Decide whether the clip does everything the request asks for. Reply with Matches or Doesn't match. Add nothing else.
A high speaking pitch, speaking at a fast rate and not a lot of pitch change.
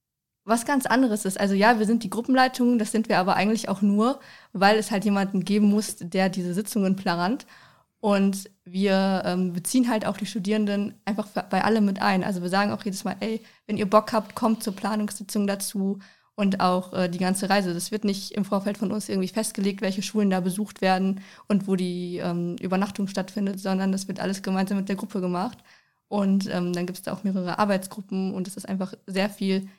Matches